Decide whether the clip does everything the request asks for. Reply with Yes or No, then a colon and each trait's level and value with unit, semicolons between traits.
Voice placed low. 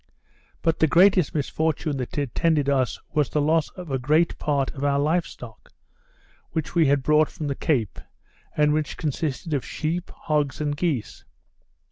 No: medium, 150 Hz